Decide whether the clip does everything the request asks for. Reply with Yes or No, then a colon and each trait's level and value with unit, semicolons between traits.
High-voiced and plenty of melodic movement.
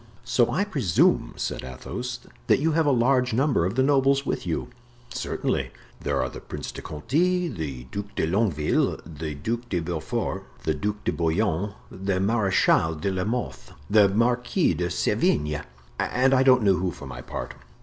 No: low, 100 Hz; wide, 7.6 semitones